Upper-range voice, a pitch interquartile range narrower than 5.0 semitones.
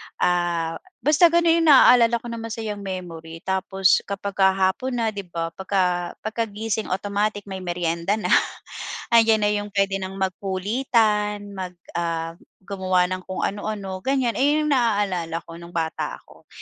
Yes: high, 195 Hz; average, 3.5 semitones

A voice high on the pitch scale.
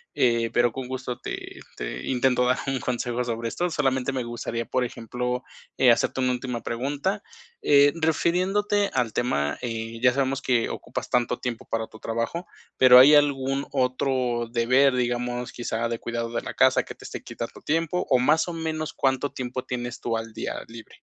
No: low, 125 Hz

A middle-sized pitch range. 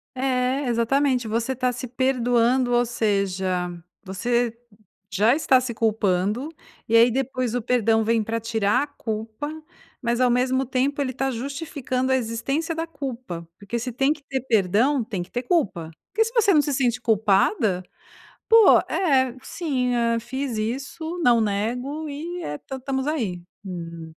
Yes: average, 3.4 semitones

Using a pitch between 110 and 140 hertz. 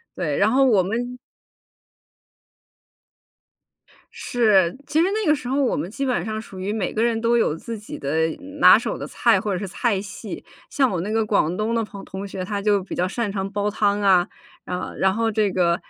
No: high, 205 Hz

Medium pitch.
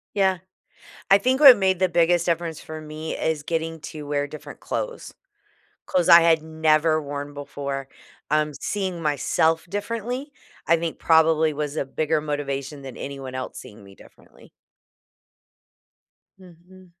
Yes: medium, 160 Hz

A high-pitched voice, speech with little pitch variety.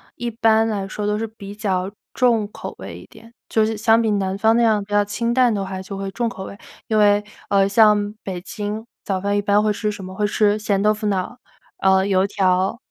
Yes: high, 205 Hz; narrow, 2.0 semitones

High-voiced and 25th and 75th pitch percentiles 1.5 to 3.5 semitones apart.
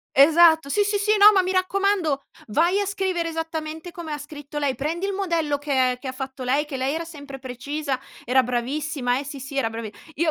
No: very high, 300 Hz; average, 4.2 semitones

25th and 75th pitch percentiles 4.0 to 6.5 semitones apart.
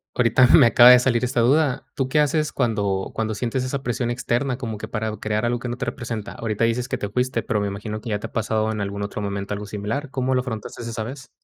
No: average, 2.9 semitones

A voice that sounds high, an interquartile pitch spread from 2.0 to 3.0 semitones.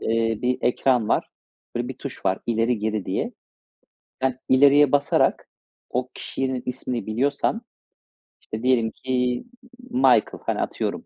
No: low, 125 Hz; narrow, 2.5 semitones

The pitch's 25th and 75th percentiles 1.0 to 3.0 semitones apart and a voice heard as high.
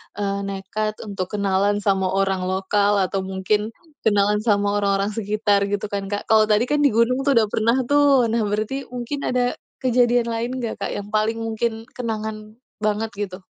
Yes: narrow, 2.4 semitones; high, 215 Hz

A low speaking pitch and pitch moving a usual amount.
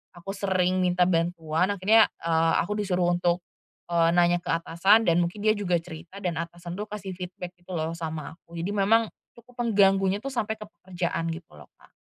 No: medium, 180 Hz; average, 3.0 semitones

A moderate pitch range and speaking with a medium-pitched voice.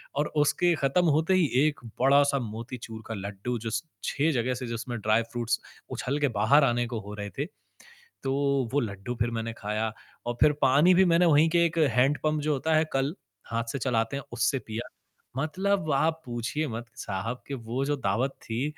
No: average, 4.6 semitones; low, 130 Hz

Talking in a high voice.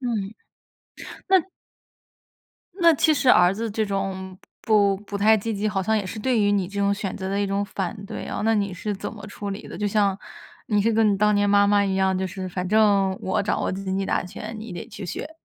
Yes: high, 200 Hz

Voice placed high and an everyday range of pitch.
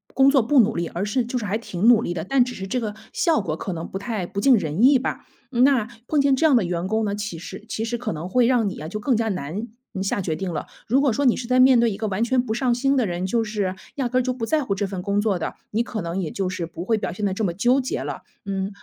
Yes: high, 215 Hz; average, 4.7 semitones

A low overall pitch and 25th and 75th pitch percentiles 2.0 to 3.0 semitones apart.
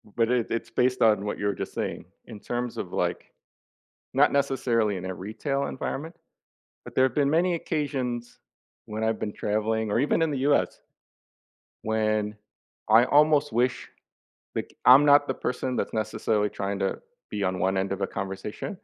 No: low, 115 Hz; average, 4.6 semitones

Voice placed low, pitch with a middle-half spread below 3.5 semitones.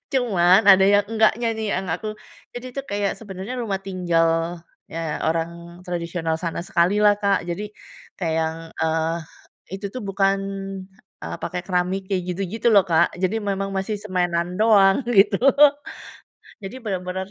No: high, 190 Hz; average, 3.0 semitones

